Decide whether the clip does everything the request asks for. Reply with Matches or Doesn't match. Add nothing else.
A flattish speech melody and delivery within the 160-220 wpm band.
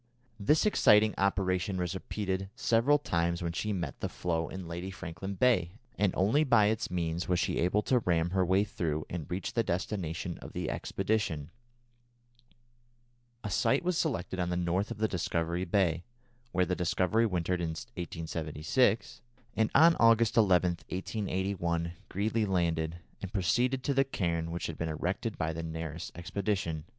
Doesn't match